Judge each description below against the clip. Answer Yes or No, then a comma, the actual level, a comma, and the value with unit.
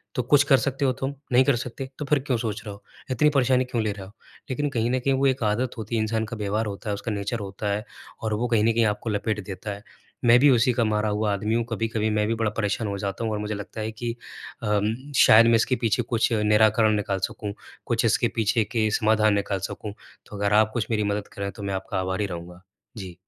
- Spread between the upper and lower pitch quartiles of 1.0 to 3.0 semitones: Yes, narrow, 2.4 semitones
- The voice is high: No, low, 110 Hz